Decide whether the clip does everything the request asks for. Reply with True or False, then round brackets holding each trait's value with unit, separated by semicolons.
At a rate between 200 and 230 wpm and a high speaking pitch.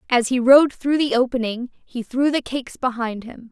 True (205 wpm; 250 Hz)